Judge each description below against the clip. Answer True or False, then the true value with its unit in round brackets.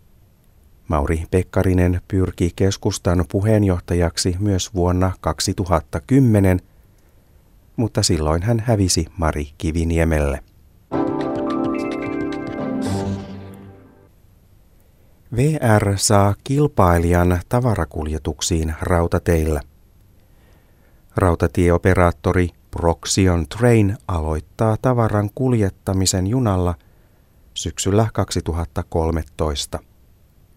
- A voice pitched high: False (90 Hz)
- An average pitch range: True (3.0 semitones)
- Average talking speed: False (55 wpm)